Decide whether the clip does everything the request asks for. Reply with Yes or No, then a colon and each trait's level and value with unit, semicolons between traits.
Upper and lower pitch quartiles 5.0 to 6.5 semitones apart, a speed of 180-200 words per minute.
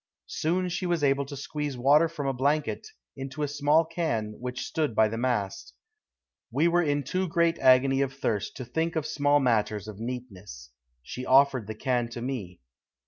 No: average, 4.3 semitones; average, 185 wpm